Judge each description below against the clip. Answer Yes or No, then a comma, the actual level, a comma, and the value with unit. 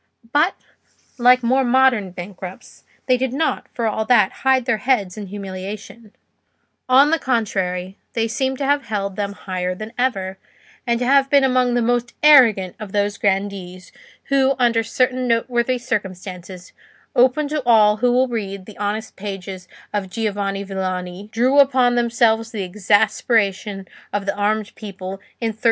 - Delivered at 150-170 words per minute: Yes, average, 155 wpm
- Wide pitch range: No, average, 4.3 semitones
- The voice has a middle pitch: No, high, 220 Hz